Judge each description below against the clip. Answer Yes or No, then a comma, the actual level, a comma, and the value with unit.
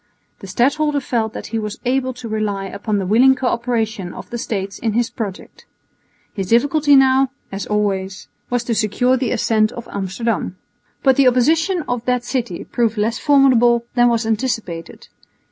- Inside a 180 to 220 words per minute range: No, average, 170 wpm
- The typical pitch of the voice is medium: No, high, 235 Hz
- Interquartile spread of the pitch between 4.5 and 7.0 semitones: No, average, 3.4 semitones